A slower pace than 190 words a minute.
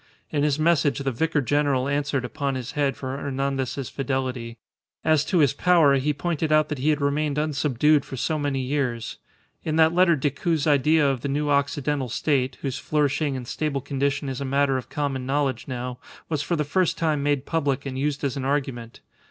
No: average, 195 wpm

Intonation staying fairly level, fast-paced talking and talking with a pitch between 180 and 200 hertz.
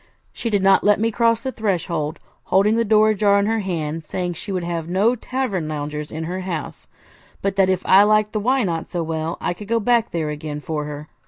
No: average, 4.8 semitones; fast, 235 wpm; high, 190 Hz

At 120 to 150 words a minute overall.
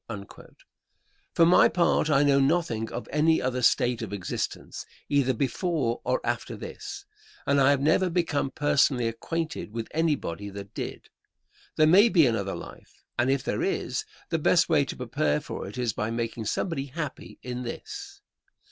No: average, 165 wpm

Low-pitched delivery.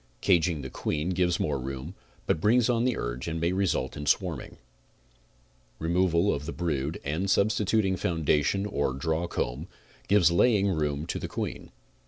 Yes: very low, 85 Hz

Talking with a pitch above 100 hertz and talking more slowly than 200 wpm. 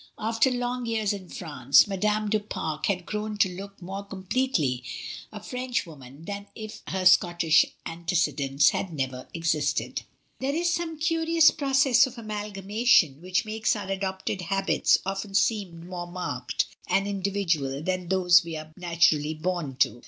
Yes: high, 190 Hz; average, 150 wpm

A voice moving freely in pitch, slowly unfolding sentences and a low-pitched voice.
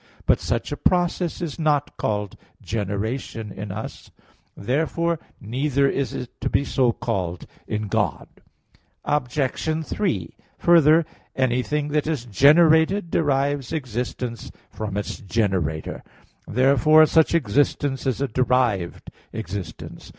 Yes: wide, 6.1 semitones; slow, 115 wpm; low, 130 Hz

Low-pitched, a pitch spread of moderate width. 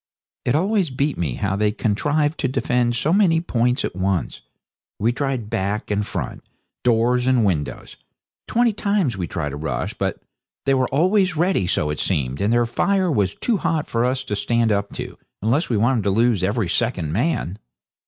No: low, 120 Hz; wide, 6.7 semitones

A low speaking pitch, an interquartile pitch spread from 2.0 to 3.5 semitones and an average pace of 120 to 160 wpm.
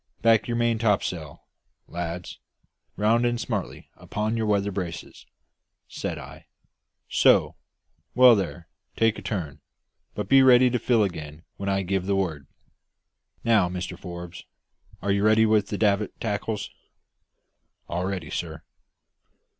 No: low, 100 Hz; average, 4.1 semitones; slow, 135 wpm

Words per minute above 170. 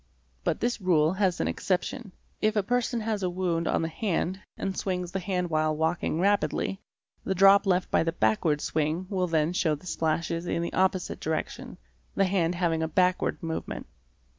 Yes: average, 185 wpm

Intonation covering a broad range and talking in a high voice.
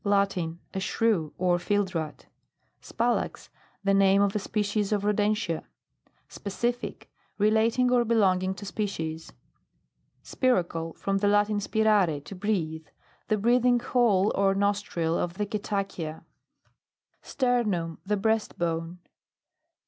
No: average, 3.3 semitones; high, 200 Hz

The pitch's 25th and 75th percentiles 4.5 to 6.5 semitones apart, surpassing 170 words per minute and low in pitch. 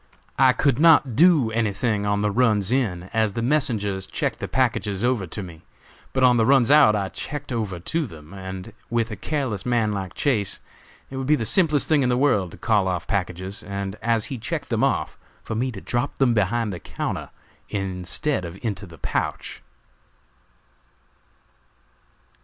Yes: average, 4.9 semitones; average, 180 wpm; low, 110 Hz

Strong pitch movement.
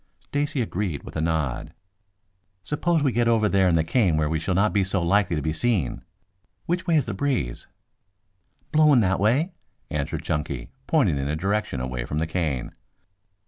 Yes: wide, 7.6 semitones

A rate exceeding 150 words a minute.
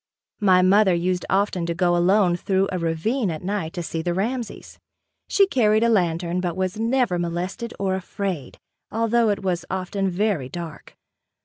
Yes: average, 170 wpm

